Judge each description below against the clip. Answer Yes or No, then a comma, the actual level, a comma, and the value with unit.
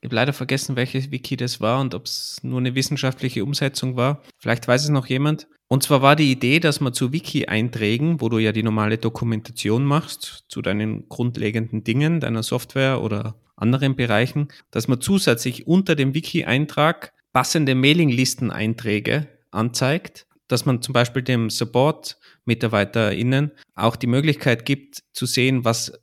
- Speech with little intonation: No, average, 3.6 semitones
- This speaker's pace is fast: No, average, 155 wpm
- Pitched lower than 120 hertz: No, low, 130 Hz